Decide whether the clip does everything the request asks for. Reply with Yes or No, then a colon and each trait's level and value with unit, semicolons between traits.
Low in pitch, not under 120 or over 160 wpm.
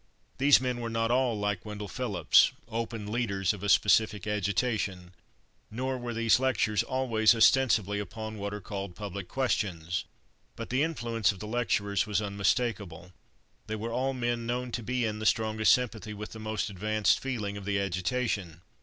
No: low, 110 Hz; average, 170 wpm